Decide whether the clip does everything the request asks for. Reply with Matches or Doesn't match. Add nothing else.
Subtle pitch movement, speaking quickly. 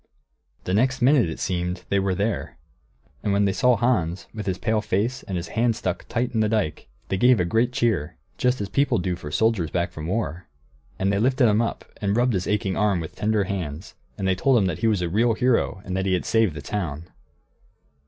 Doesn't match